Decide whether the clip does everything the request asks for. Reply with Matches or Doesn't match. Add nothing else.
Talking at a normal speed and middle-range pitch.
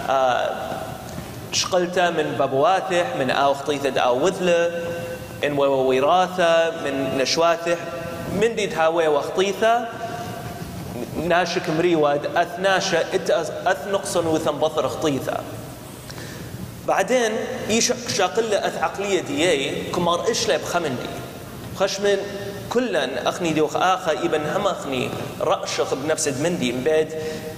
Doesn't match